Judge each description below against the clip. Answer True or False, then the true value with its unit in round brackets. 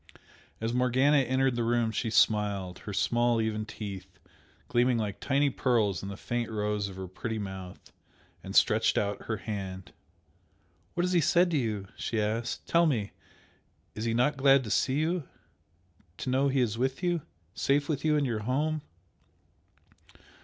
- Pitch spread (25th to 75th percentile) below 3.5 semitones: False (4.5 semitones)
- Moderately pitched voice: False (120 Hz)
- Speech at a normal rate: True (165 wpm)